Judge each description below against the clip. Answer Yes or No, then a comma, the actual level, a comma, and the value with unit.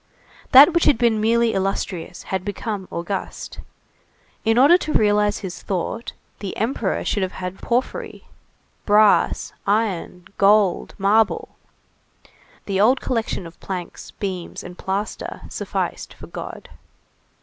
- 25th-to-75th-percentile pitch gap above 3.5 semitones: No, average, 2.9 semitones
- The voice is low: No, high, 205 Hz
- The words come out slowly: Yes, slow, 125 wpm